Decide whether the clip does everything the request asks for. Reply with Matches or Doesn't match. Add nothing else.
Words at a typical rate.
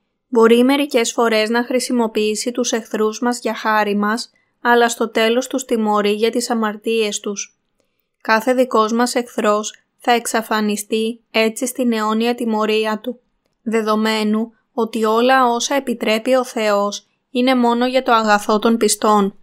Matches